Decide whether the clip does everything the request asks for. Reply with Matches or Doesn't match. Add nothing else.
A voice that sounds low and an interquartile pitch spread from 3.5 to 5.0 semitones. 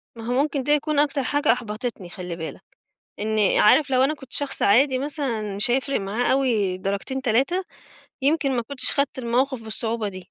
Doesn't match